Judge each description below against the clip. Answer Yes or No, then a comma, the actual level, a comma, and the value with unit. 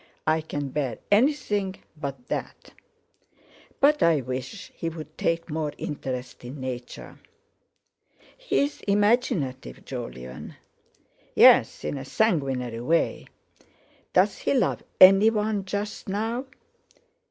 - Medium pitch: Yes, medium, 160 Hz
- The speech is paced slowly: Yes, slow, 100 wpm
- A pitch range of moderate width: No, wide, 8.1 semitones